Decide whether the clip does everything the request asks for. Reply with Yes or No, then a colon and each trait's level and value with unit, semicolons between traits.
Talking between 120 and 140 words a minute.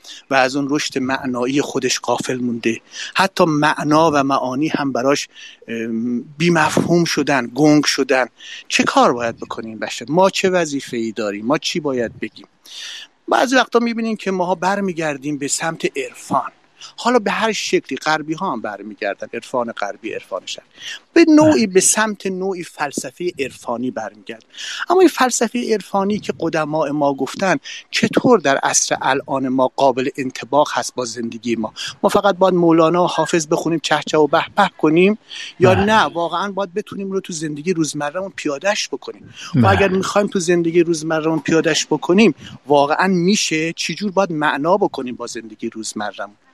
No: fast, 155 wpm